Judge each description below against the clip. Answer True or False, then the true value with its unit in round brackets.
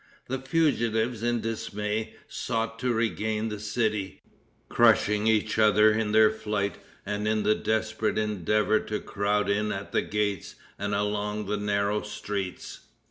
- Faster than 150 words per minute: False (140 wpm)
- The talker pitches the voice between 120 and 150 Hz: False (105 Hz)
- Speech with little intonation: True (1.2 semitones)